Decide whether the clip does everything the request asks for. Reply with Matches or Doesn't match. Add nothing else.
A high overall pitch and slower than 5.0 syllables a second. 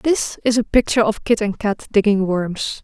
Matches